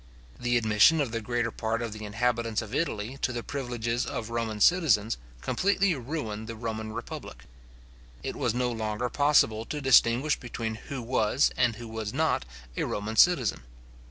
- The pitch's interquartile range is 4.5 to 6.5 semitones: No, average, 2.7 semitones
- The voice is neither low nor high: No, low, 115 Hz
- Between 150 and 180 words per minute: Yes, average, 165 wpm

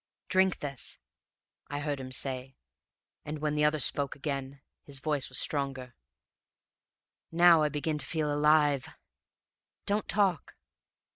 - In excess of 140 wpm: No, slow, 135 wpm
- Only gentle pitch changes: Yes, narrow, 2.1 semitones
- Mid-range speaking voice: Yes, medium, 145 Hz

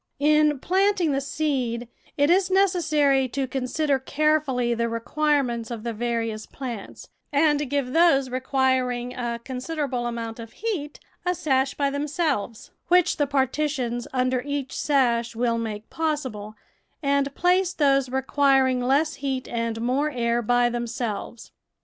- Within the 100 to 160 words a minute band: Yes, slow, 135 wpm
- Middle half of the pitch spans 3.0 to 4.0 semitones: Yes, average, 3.7 semitones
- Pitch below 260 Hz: No, very high, 265 Hz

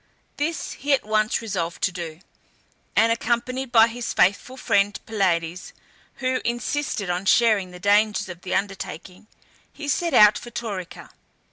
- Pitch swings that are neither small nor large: Yes, average, 4.5 semitones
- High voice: Yes, high, 215 Hz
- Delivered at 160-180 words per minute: No, average, 145 wpm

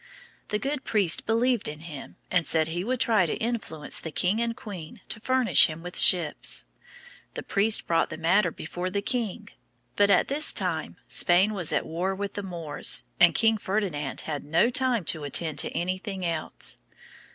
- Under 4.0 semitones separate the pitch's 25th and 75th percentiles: No, average, 5.0 semitones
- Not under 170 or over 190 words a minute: Yes, average, 180 wpm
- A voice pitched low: No, medium, 185 Hz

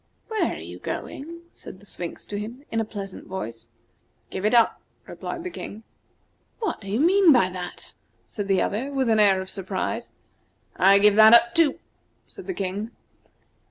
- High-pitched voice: Yes, high, 215 Hz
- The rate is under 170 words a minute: No, average, 180 wpm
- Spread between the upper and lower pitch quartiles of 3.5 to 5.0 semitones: No, wide, 5.4 semitones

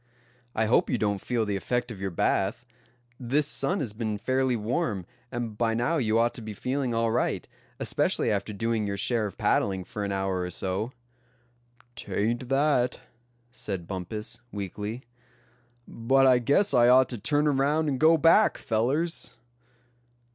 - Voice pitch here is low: Yes, low, 115 Hz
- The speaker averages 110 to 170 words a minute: Yes, average, 160 wpm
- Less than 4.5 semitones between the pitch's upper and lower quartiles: Yes, average, 4.1 semitones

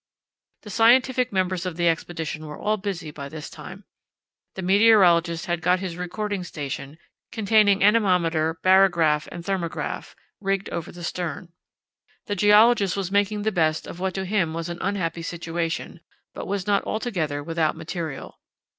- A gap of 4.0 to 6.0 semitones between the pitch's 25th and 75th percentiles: No, average, 3.5 semitones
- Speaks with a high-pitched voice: No, medium, 180 Hz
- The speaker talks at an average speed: Yes, average, 155 wpm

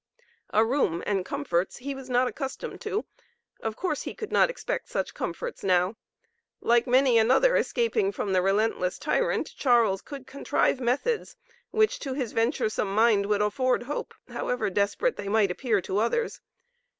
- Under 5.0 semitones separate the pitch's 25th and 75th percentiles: No, wide, 5.6 semitones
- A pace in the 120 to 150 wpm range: No, average, 160 wpm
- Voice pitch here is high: Yes, high, 240 Hz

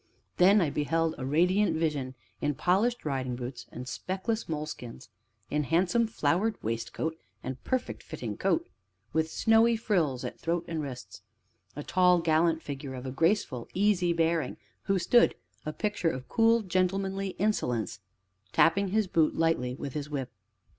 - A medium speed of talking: Yes, average, 150 wpm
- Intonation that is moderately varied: No, wide, 5.8 semitones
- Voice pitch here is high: No, medium, 165 Hz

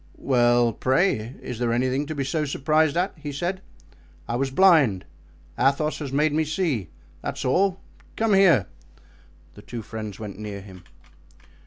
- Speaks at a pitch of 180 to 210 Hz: No, low, 135 Hz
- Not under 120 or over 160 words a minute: Yes, average, 155 wpm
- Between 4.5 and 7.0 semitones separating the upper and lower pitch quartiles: Yes, average, 5.2 semitones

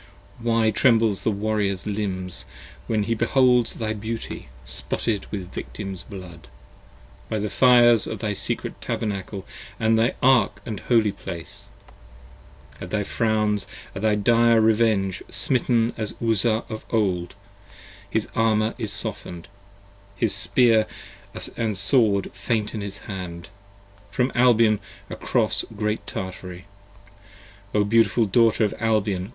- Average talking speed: No, slow, 125 wpm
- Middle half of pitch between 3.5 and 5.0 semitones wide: No, narrow, 2.6 semitones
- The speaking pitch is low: Yes, low, 110 Hz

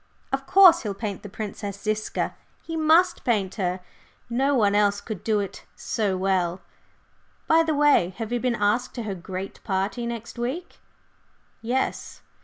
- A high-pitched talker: Yes, high, 215 Hz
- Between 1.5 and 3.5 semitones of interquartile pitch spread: No, average, 4.7 semitones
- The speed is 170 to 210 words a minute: No, average, 160 wpm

